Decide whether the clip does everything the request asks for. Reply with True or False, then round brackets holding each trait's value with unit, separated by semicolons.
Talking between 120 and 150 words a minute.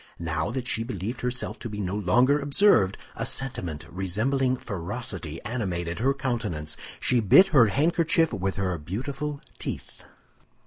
True (140 wpm)